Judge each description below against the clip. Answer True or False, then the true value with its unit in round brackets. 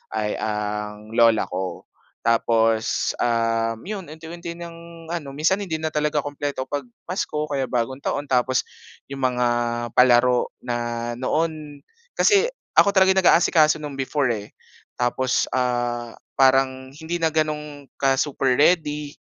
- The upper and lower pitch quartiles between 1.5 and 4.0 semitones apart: False (4.6 semitones)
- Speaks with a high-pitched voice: False (135 Hz)